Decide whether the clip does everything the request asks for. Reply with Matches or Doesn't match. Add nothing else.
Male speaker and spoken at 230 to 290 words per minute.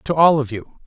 Matches